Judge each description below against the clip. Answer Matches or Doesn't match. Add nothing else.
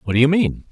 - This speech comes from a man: Matches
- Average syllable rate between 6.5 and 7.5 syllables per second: Matches